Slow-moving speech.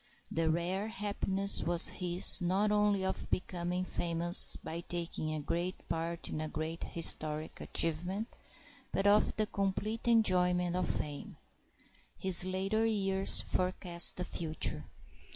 Yes: slow, 130 wpm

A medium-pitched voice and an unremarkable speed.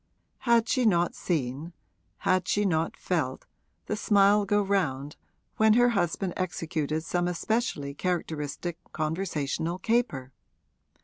No: medium, 175 Hz; slow, 115 wpm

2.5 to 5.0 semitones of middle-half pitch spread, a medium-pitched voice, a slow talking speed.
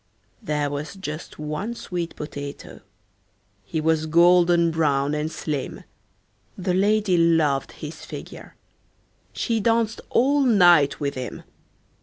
Yes: average, 4.2 semitones; medium, 165 Hz; slow, 115 wpm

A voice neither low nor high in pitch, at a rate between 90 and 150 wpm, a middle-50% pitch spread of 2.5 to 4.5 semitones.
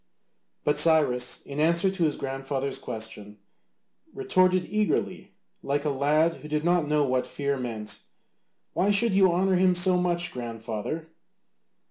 No: medium, 150 Hz; average, 145 wpm; average, 5.0 semitones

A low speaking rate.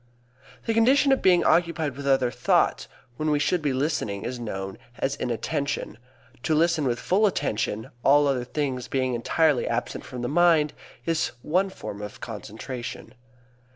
No: average, 155 wpm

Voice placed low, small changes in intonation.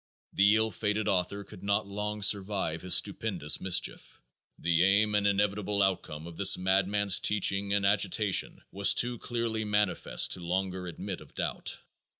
Yes: low, 100 Hz; narrow, 1.9 semitones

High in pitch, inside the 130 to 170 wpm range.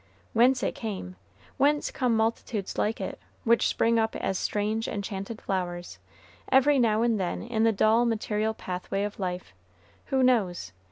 Yes: high, 220 Hz; average, 155 wpm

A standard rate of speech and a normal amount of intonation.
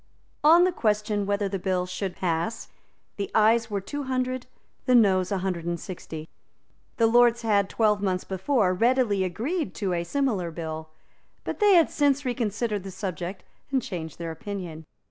Yes: average, 165 wpm; average, 4.9 semitones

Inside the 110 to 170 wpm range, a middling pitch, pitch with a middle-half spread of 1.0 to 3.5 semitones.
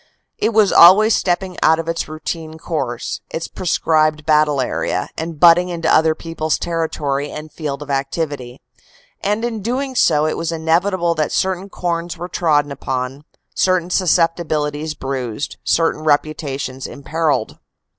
Yes: average, 145 wpm; medium, 160 Hz; average, 2.9 semitones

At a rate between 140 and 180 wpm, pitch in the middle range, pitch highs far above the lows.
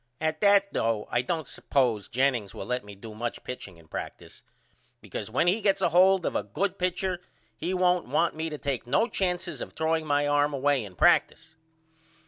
No: average, 195 wpm; medium, 145 Hz; wide, 6.8 semitones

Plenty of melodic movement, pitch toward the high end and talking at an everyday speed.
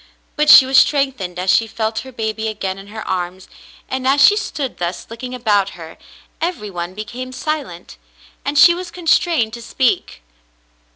Yes: wide, 6.0 semitones; high, 230 Hz; average, 170 wpm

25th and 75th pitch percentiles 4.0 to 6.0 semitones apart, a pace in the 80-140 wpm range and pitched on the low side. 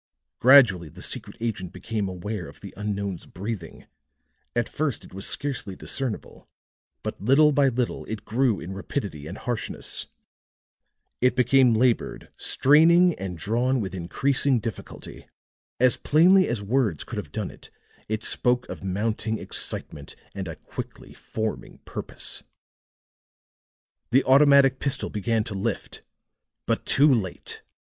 Yes: average, 5.3 semitones; slow, 135 wpm; low, 115 Hz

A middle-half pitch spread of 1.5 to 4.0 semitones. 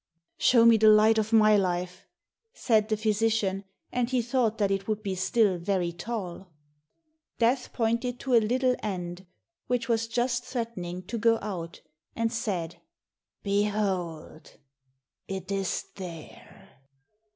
Yes: average, 3.5 semitones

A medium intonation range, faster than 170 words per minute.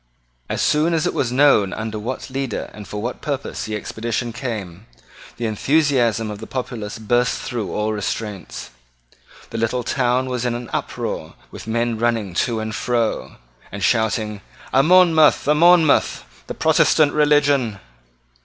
No: average, 4.0 semitones; average, 155 wpm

